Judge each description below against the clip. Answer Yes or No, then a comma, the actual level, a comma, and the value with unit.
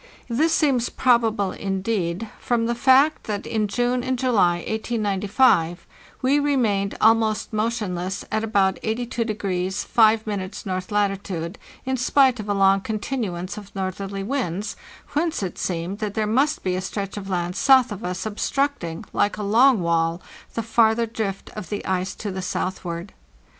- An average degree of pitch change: Yes, average, 3.7 semitones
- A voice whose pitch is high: Yes, high, 210 Hz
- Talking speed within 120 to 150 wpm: No, average, 160 wpm